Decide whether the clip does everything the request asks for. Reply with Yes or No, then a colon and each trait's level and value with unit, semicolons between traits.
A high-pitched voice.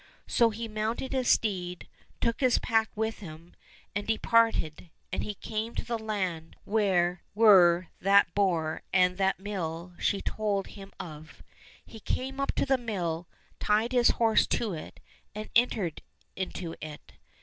Yes: high, 205 Hz